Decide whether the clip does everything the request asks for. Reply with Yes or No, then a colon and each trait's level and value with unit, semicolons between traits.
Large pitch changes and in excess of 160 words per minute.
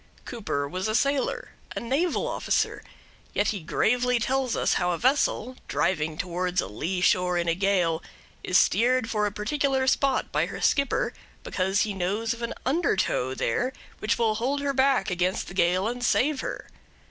Yes: wide, 6.1 semitones; average, 175 wpm